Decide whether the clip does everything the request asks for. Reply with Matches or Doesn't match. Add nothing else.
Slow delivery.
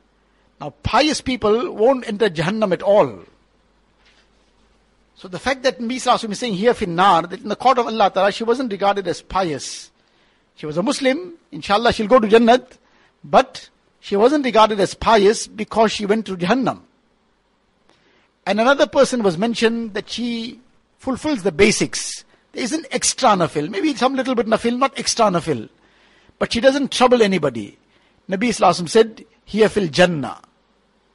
Doesn't match